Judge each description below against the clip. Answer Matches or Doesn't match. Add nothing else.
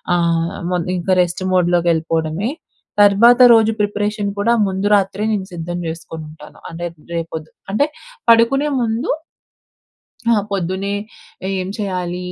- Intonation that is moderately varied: Matches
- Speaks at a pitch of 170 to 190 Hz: Matches